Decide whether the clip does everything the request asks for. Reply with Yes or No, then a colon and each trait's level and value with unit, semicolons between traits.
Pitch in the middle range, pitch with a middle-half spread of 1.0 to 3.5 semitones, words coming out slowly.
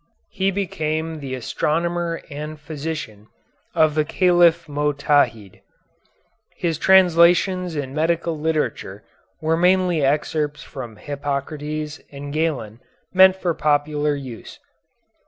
Yes: medium, 155 Hz; average, 2.8 semitones; slow, 100 wpm